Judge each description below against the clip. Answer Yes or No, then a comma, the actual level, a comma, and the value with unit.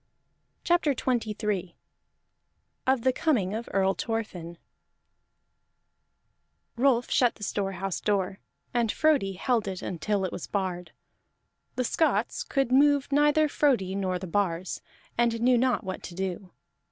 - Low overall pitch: No, high, 210 Hz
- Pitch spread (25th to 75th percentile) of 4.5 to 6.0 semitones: Yes, average, 5.2 semitones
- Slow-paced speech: Yes, slow, 130 wpm